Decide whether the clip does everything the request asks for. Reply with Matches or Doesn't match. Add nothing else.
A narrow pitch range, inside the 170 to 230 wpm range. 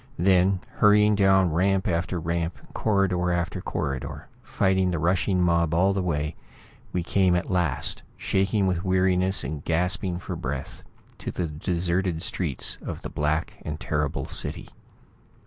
Doesn't match